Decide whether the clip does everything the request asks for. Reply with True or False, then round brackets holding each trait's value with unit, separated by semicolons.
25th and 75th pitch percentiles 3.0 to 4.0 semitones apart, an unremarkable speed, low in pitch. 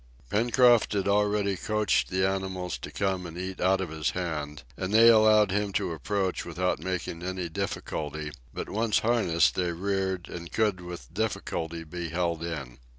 True (3.3 semitones; 165 wpm; 95 Hz)